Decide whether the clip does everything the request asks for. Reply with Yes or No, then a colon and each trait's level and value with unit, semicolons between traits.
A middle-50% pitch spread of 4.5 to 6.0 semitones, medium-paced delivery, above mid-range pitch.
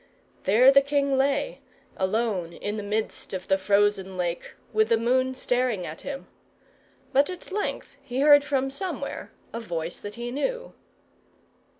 Yes: wide, 5.5 semitones; average, 155 wpm; high, 240 Hz